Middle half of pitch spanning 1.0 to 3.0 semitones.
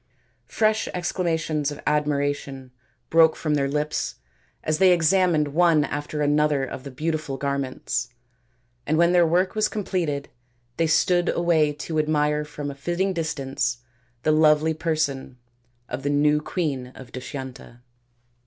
Yes: average, 2.7 semitones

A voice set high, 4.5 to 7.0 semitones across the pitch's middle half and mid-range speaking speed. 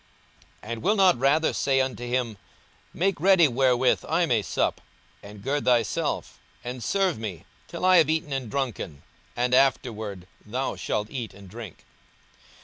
No: low, 125 Hz; average, 5.2 semitones; average, 155 wpm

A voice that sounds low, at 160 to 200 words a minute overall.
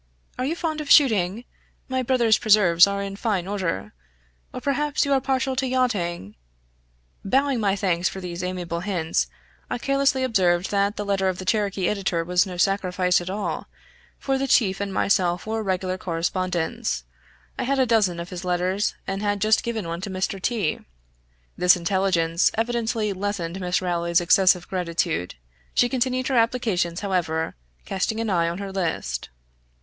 No: high, 195 Hz; average, 170 wpm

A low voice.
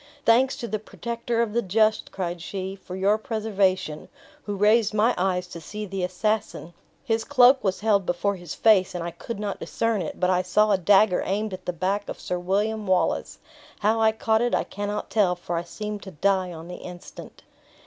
No: high, 200 Hz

